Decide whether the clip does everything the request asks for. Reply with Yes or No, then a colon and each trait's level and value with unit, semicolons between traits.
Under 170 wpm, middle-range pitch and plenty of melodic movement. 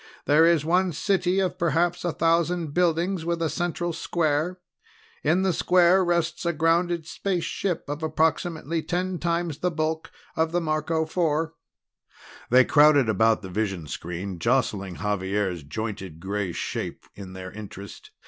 Yes: average, 145 wpm; medium, 160 Hz; wide, 7.9 semitones